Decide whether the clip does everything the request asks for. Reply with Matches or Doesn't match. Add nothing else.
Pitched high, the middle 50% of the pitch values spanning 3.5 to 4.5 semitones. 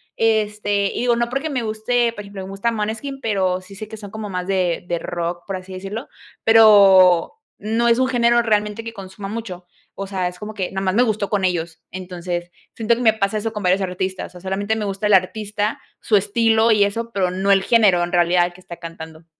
Doesn't match